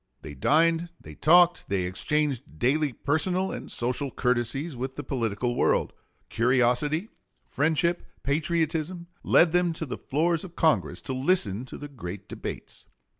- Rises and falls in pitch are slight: No, average, 5.2 semitones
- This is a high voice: No, medium, 145 Hz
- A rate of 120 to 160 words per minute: Yes, average, 140 wpm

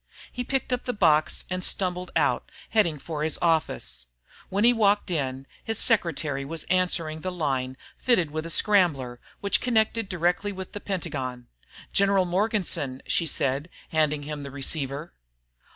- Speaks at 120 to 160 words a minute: Yes, average, 150 wpm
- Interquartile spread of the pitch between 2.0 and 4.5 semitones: No, wide, 5.5 semitones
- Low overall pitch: No, medium, 170 Hz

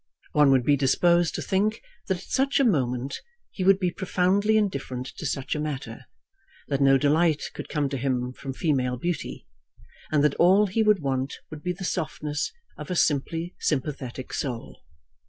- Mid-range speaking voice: Yes, medium, 150 Hz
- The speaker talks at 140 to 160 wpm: No, average, 175 wpm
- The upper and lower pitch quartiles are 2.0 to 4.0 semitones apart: No, average, 5.1 semitones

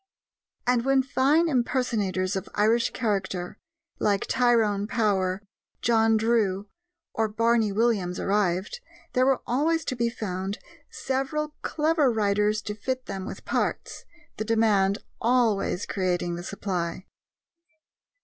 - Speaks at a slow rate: Yes, slow, 120 wpm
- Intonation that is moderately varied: Yes, average, 4.0 semitones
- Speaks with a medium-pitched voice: No, high, 220 Hz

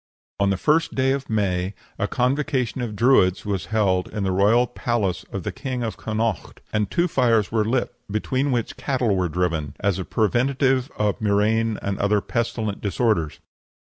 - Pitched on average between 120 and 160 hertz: No, low, 110 Hz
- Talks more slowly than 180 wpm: Yes, average, 170 wpm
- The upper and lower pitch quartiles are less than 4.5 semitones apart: Yes, average, 4.0 semitones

